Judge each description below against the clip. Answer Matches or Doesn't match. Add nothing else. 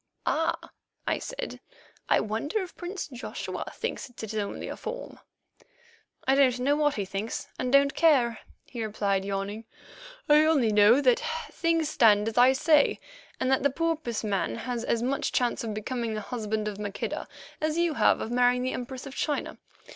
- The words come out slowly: Doesn't match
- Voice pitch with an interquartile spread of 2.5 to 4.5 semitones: Doesn't match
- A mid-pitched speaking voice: Doesn't match